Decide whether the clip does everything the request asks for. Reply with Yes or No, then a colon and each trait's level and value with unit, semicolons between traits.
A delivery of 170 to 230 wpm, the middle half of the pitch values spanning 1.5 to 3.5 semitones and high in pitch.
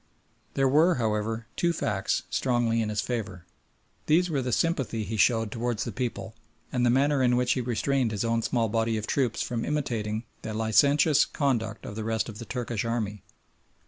No: average, 185 wpm; average, 2.9 semitones; low, 115 Hz